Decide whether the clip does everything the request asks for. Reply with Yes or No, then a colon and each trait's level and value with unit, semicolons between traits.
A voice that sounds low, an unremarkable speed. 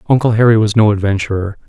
Yes: low, 105 Hz; average, 180 wpm